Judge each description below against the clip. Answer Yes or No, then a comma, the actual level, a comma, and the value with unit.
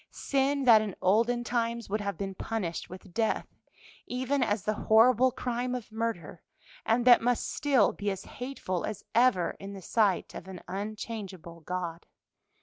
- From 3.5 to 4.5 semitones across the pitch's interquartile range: Yes, average, 4.1 semitones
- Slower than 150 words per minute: No, average, 160 wpm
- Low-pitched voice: No, high, 220 Hz